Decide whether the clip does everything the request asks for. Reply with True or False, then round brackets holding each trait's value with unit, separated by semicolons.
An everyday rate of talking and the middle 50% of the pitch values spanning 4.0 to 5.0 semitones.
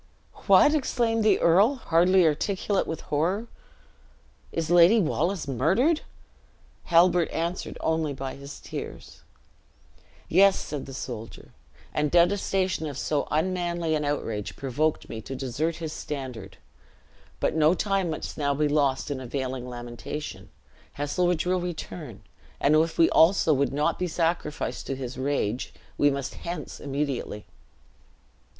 False (130 wpm; 4.3 semitones)